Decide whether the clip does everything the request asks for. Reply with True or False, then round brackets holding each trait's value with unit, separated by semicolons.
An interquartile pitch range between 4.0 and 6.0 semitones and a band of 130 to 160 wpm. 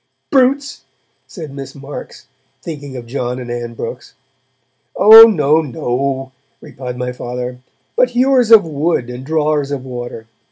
True (4.7 semitones; 135 wpm)